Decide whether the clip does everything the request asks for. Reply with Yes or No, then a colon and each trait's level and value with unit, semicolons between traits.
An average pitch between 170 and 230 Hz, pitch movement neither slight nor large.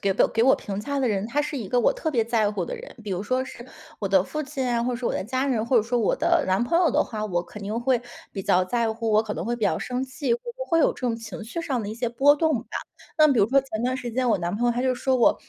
No: high, 240 Hz; average, 3.5 semitones